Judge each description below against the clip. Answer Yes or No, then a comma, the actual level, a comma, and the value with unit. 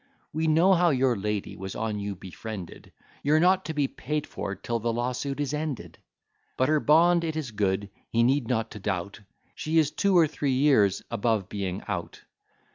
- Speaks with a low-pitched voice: Yes, low, 125 Hz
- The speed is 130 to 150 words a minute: No, average, 190 wpm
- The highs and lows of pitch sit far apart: Yes, wide, 7.0 semitones